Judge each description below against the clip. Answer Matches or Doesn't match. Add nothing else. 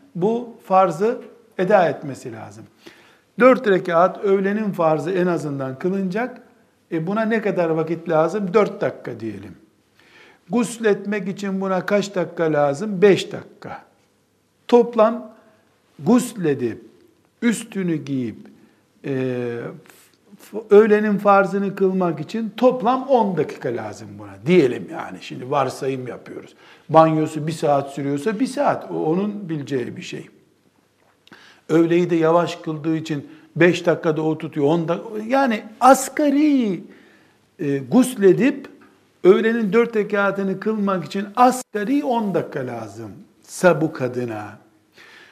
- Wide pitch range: Matches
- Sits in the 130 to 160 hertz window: Doesn't match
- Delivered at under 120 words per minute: Matches